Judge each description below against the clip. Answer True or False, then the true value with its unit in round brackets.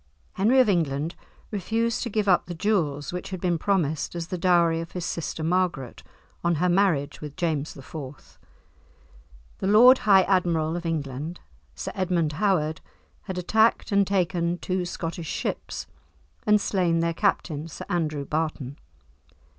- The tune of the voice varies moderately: True (3.4 semitones)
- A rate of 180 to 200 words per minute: False (150 wpm)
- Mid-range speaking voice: True (175 Hz)